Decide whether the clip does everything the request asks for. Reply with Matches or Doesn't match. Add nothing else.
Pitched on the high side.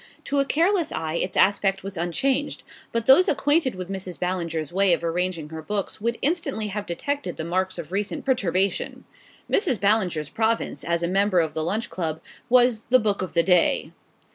Matches